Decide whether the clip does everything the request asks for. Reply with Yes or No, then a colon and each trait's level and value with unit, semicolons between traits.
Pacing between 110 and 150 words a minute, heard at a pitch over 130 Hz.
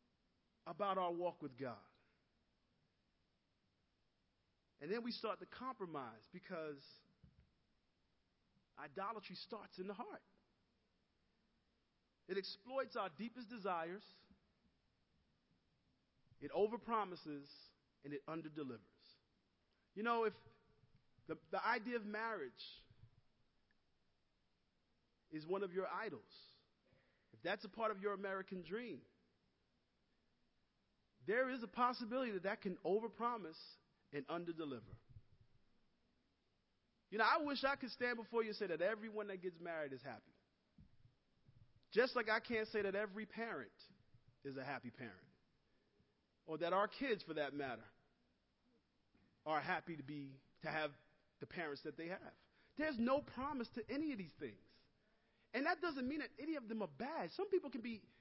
Yes: slow, 135 wpm; medium, 185 Hz